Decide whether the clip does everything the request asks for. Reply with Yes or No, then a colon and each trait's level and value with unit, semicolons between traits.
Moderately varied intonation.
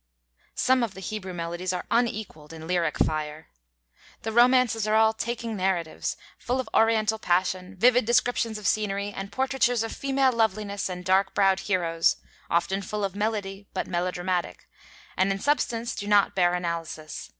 Yes: average, 3.9 semitones